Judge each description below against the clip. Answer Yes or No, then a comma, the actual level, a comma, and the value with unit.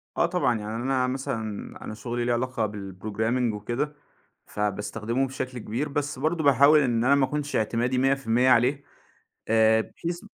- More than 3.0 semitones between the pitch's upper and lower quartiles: Yes, average, 3.6 semitones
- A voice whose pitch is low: Yes, low, 125 Hz